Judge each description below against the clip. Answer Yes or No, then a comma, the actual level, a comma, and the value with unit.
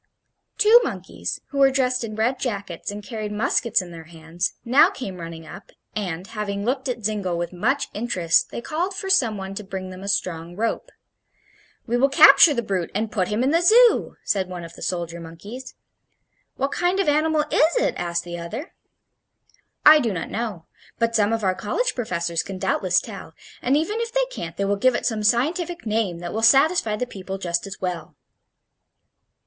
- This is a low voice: No, high, 215 Hz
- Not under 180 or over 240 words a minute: Yes, average, 195 wpm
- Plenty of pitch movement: Yes, wide, 6.5 semitones